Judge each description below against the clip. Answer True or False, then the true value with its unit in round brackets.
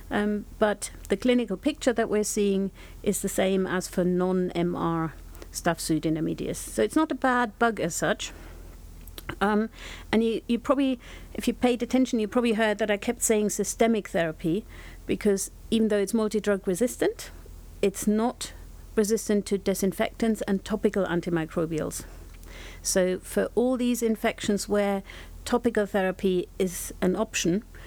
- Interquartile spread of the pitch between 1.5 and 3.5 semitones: False (4.0 semitones)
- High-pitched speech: True (205 Hz)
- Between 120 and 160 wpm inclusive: True (145 wpm)